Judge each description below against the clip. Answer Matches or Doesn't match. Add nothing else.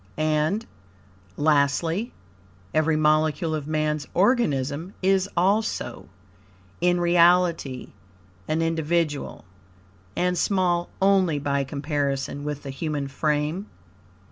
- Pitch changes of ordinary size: Matches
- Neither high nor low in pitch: Matches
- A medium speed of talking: Doesn't match